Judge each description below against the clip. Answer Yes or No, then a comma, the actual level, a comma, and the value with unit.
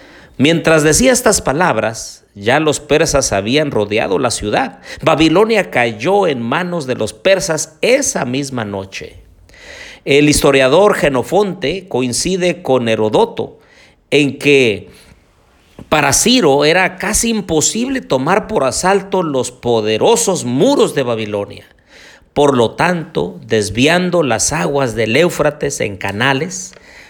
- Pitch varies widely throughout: Yes, wide, 7.2 semitones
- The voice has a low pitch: No, medium, 145 Hz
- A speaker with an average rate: No, slow, 115 wpm